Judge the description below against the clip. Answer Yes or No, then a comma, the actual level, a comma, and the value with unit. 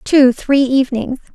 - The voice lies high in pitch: Yes, very high, 260 Hz